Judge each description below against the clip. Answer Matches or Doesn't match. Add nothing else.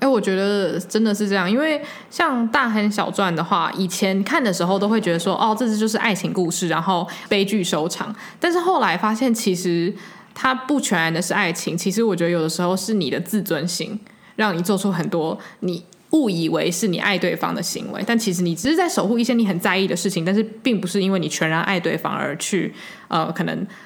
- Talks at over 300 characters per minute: Matches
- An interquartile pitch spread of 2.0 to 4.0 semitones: Matches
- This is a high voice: Matches